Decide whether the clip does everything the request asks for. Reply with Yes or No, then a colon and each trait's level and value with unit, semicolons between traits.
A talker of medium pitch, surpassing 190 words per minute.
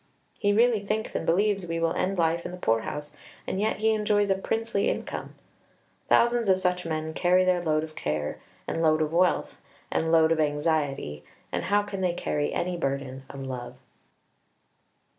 No: medium, 170 Hz; average, 180 wpm